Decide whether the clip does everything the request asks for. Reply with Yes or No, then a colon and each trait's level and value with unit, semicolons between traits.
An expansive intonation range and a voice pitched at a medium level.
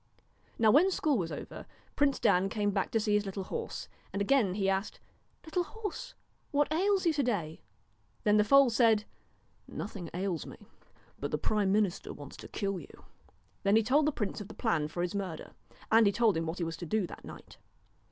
No: wide, 5.8 semitones; high, 210 Hz